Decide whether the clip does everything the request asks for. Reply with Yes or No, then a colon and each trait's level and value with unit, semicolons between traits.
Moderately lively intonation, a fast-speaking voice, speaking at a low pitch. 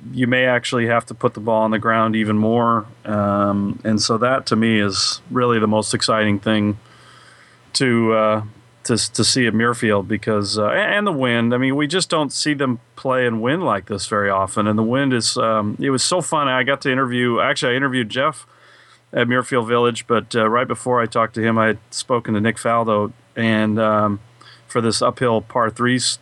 No: narrow, 2.3 semitones; fast, 215 wpm; low, 115 Hz